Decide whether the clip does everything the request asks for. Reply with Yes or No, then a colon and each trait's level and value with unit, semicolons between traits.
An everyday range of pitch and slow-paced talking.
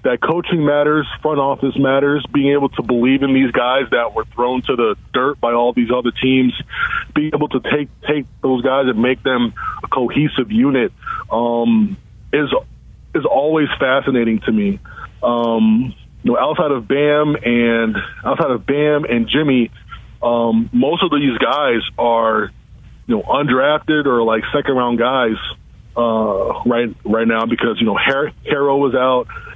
No: average, 3.8 semitones; average, 165 wpm